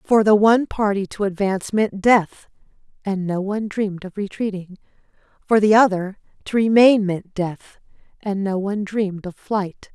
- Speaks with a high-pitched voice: Yes, high, 200 Hz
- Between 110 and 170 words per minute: Yes, average, 165 wpm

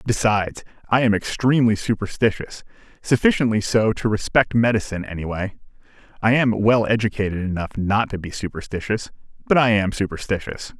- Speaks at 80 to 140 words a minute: Yes, slow, 135 wpm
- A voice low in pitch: Yes, low, 105 Hz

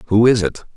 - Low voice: Yes, low, 110 Hz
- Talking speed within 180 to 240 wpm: Yes, fast, 235 wpm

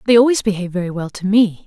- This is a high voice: Yes, high, 200 Hz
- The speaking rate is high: Yes, fast, 250 wpm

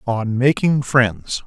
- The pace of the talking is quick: No, slow, 125 wpm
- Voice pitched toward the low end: Yes, low, 120 Hz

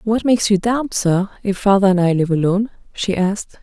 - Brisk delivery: Yes, fast, 215 wpm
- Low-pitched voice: No, high, 200 Hz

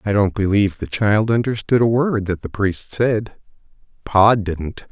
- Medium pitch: No, low, 105 Hz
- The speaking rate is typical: Yes, average, 170 wpm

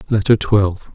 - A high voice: No, low, 100 Hz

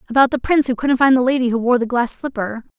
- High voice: Yes, very high, 250 Hz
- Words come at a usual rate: No, fast, 280 wpm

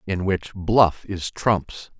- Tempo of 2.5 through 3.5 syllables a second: Yes, 3.1 syllables/s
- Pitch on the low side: Yes, very low, 95 Hz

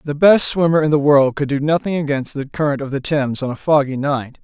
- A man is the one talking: Yes, male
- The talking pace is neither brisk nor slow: No, fast, 255 wpm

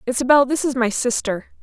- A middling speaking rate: Yes, average, 185 wpm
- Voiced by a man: No, female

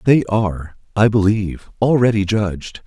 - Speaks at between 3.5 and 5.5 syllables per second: Yes, 5.0 syllables/s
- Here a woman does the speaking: No, male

